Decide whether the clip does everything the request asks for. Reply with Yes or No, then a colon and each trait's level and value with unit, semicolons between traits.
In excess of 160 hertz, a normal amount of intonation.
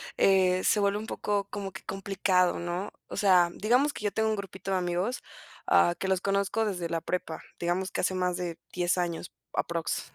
No: high, 190 Hz; narrow, 2.2 semitones